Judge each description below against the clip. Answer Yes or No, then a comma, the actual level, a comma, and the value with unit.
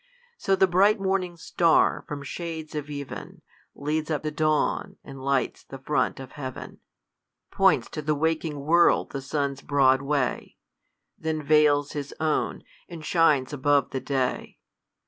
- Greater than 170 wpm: No, average, 145 wpm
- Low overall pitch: No, medium, 150 Hz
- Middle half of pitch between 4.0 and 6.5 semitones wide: No, narrow, 2.5 semitones